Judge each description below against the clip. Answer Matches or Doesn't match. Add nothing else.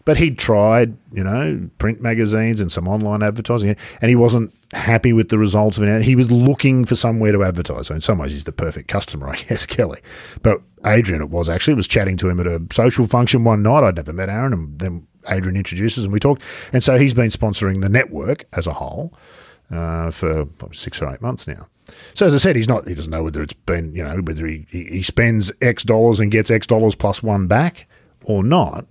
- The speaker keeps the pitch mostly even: Doesn't match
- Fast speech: Matches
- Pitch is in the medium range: Doesn't match